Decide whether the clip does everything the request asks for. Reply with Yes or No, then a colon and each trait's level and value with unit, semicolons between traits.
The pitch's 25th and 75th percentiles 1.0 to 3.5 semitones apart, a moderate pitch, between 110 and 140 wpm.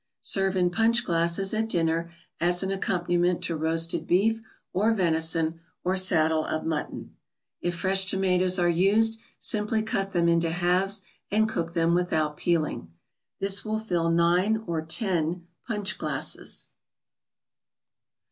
Yes: average, 2.8 semitones; medium, 180 Hz; slow, 135 wpm